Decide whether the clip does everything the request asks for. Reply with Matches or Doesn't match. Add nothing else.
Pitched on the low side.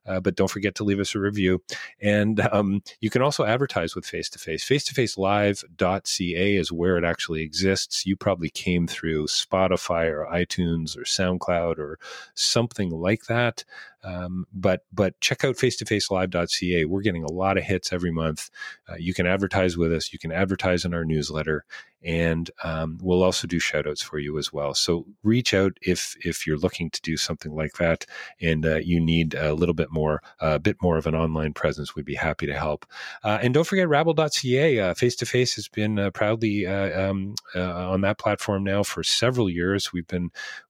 Matches